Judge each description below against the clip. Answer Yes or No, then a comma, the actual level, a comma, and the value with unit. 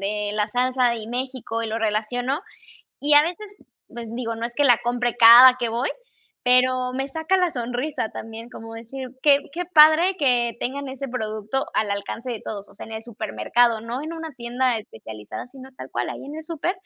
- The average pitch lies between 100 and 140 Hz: No, high, 245 Hz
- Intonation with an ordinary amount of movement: Yes, average, 3.3 semitones